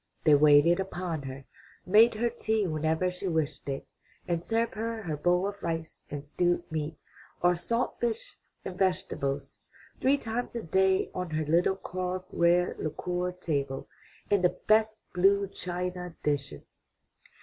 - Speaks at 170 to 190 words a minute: No, average, 150 wpm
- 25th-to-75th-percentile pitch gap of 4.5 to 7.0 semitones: No, average, 3.9 semitones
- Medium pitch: Yes, medium, 180 Hz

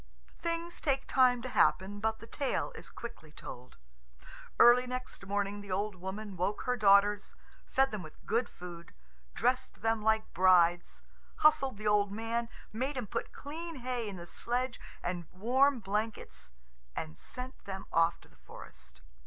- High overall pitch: Yes, high, 215 Hz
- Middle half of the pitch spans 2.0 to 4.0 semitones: No, average, 4.8 semitones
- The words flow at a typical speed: Yes, average, 160 wpm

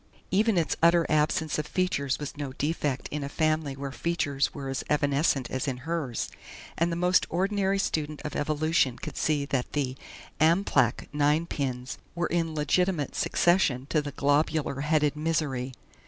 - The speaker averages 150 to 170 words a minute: Yes, average, 155 wpm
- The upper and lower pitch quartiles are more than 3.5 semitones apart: No, average, 3.1 semitones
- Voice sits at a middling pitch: Yes, medium, 150 Hz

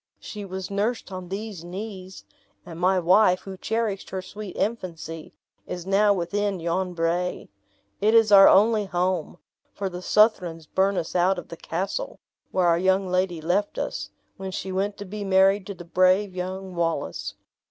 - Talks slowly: No, average, 170 wpm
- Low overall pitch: No, high, 190 Hz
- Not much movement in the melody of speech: Yes, narrow, 2.1 semitones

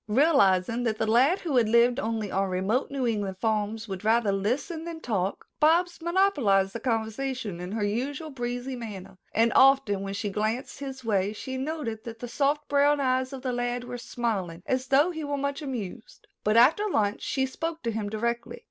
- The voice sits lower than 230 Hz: No, high, 240 Hz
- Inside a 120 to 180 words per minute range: No, average, 195 wpm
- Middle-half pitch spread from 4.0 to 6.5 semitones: Yes, average, 4.4 semitones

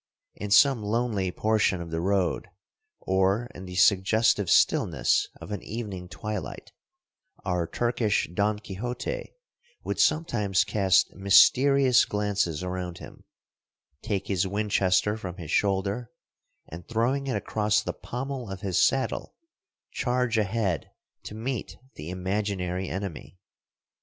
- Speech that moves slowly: Yes, slow, 120 wpm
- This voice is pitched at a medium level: No, low, 100 Hz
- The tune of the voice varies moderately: Yes, average, 3.7 semitones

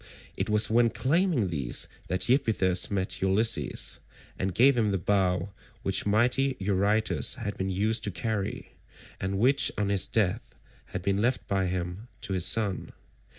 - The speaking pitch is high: No, low, 100 Hz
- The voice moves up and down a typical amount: Yes, average, 3.3 semitones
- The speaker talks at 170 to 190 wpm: No, average, 155 wpm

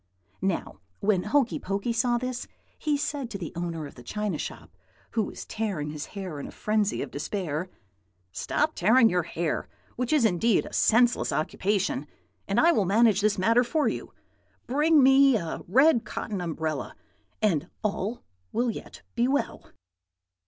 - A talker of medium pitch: No, high, 215 Hz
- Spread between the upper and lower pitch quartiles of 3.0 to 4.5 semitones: No, wide, 5.6 semitones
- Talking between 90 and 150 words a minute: No, average, 160 wpm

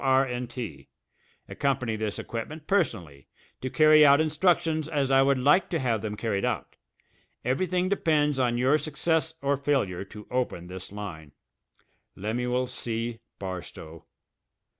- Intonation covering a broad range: Yes, wide, 6.1 semitones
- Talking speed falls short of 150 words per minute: Yes, average, 140 wpm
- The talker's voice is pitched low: Yes, low, 130 Hz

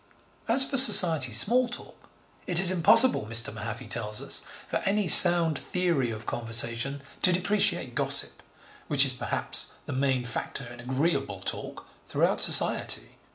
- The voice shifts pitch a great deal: Yes, wide, 7.4 semitones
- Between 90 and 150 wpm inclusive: Yes, average, 145 wpm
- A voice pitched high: No, medium, 140 Hz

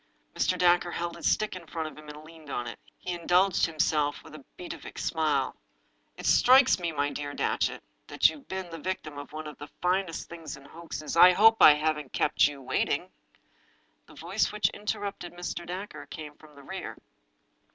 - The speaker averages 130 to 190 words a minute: No, average, 200 wpm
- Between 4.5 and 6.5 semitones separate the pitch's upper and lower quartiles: No, average, 3.2 semitones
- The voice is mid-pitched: Yes, medium, 160 Hz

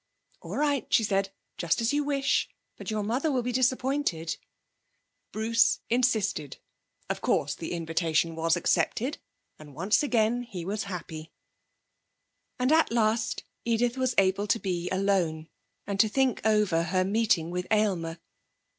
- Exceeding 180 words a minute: No, average, 145 wpm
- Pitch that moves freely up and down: Yes, wide, 6.0 semitones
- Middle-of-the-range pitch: No, high, 210 Hz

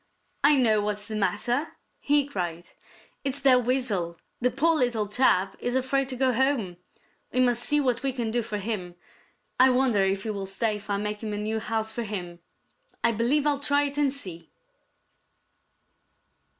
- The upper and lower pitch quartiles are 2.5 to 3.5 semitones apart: No, average, 4.3 semitones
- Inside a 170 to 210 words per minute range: Yes, average, 175 wpm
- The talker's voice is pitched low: No, high, 235 Hz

